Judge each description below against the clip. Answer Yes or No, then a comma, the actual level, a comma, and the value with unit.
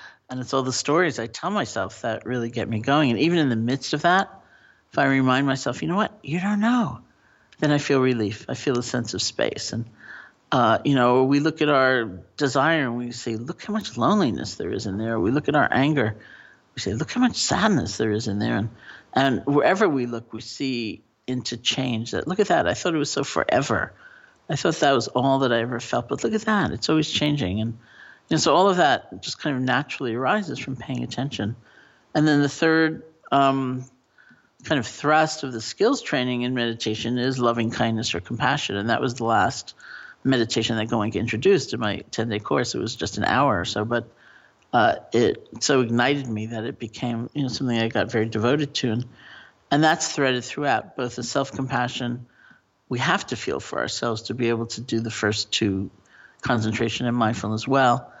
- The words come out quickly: Yes, fast, 215 wpm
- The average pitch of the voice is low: Yes, low, 125 Hz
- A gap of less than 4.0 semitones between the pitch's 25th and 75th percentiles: Yes, average, 3.6 semitones